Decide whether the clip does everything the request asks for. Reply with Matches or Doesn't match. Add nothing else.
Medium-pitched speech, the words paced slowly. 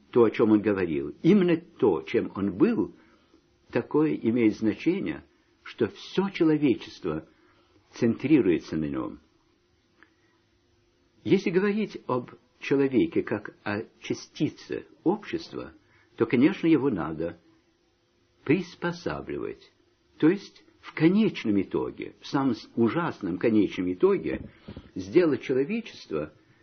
Matches